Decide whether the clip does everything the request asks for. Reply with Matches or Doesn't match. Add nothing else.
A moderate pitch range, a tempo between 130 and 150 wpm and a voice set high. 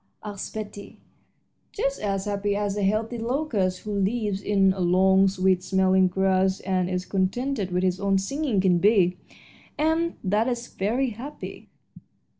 Matches